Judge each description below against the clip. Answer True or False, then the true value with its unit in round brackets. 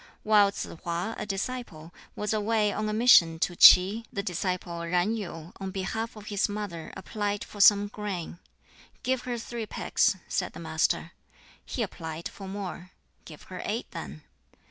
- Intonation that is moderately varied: True (3.2 semitones)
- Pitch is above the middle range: True (200 Hz)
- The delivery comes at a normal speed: True (165 wpm)